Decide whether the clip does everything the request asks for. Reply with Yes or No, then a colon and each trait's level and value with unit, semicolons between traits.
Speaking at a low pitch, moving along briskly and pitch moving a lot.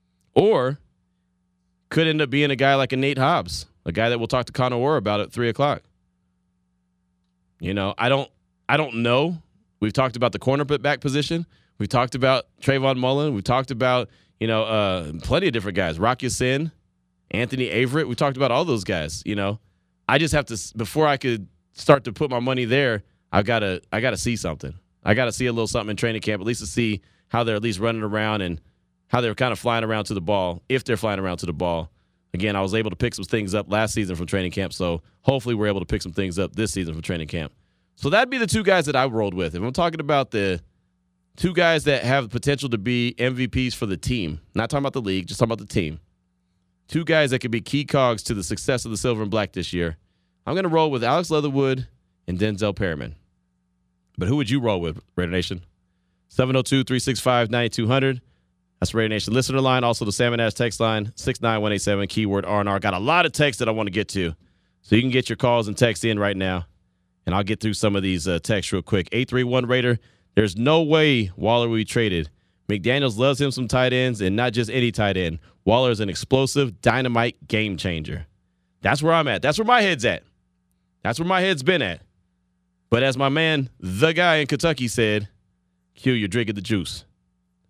Yes: low, 110 Hz; fast, 225 wpm; wide, 6.0 semitones